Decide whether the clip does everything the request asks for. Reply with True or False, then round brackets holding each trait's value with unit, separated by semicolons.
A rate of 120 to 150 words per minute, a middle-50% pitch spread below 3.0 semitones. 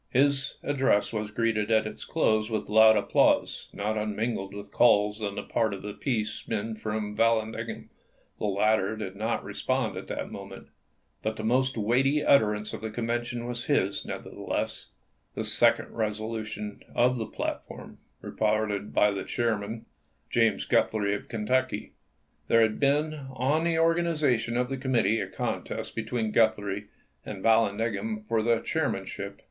False (160 wpm; 2.5 semitones)